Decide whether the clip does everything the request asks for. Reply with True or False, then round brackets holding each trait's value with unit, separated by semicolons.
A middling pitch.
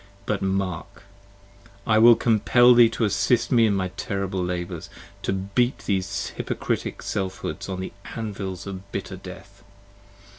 False (100 Hz)